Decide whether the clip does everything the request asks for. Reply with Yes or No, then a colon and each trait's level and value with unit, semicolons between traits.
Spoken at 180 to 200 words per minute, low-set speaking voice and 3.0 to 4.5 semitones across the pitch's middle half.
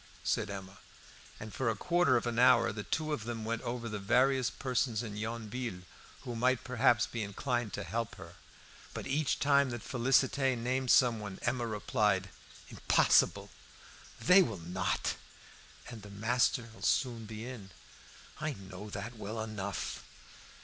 No: average, 150 wpm; low, 115 Hz; average, 3.4 semitones